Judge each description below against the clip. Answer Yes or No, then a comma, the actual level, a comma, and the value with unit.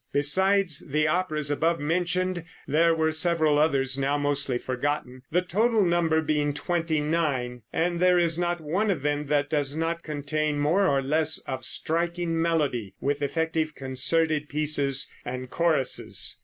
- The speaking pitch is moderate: Yes, medium, 155 Hz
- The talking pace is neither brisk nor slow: Yes, average, 150 wpm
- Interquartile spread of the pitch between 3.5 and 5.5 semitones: No, average, 2.8 semitones